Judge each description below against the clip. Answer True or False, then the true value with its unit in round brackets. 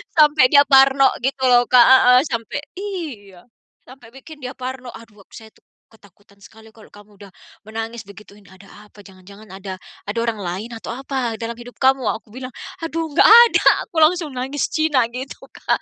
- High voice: True (240 Hz)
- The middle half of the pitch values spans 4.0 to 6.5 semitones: True (4.4 semitones)